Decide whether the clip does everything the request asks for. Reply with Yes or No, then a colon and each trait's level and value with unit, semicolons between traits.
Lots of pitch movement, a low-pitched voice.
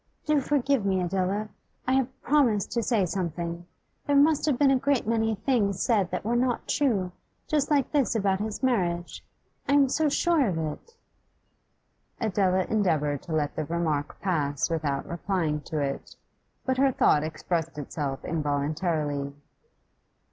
No: wide, 8.1 semitones; high, 195 Hz